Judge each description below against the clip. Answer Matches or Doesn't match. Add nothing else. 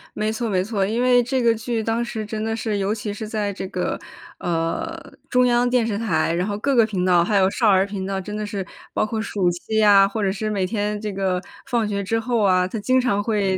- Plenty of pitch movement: Doesn't match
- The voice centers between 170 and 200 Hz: Doesn't match